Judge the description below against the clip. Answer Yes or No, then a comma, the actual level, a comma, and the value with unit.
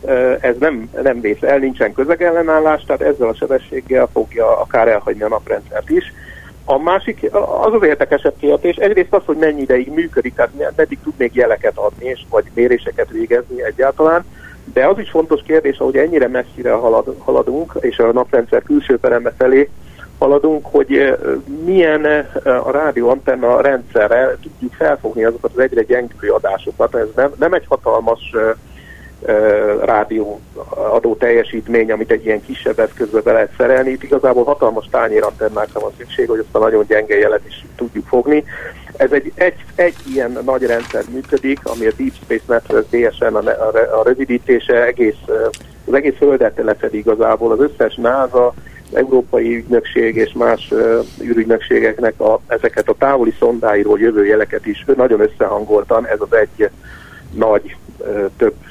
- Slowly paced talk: No, fast, 155 wpm